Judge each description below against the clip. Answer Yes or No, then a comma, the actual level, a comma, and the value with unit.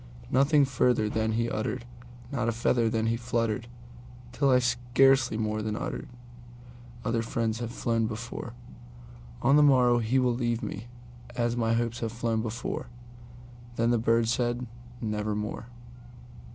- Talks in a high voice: No, low, 120 Hz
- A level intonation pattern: Yes, narrow, 1.3 semitones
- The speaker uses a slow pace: Yes, slow, 130 wpm